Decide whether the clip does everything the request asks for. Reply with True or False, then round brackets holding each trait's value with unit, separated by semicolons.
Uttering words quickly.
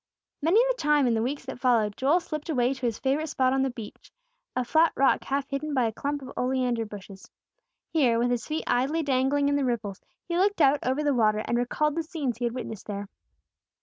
True (225 wpm)